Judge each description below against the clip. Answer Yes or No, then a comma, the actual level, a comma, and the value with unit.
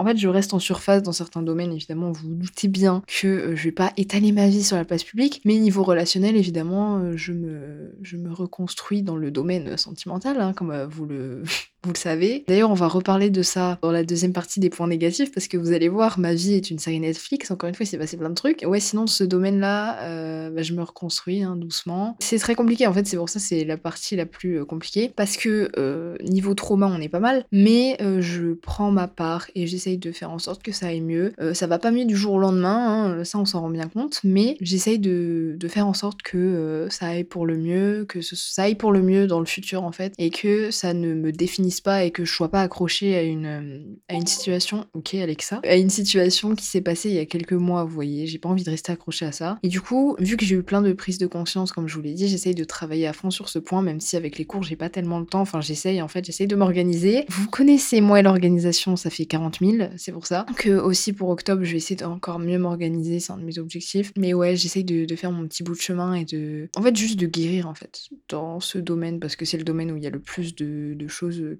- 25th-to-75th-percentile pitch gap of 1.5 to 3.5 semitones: Yes, average, 2.9 semitones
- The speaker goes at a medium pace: No, fast, 270 wpm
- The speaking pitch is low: No, medium, 180 Hz